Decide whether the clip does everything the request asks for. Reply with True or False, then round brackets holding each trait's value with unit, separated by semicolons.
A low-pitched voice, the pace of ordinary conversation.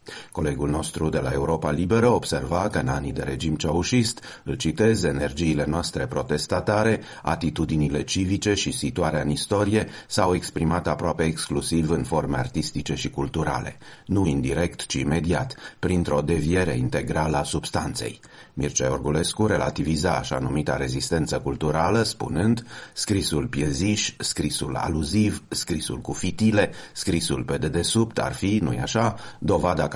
True (80 Hz; 130 wpm)